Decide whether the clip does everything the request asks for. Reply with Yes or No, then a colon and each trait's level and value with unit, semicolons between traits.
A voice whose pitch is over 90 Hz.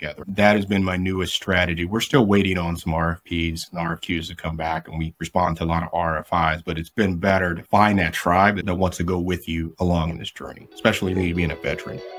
No: very low, 85 Hz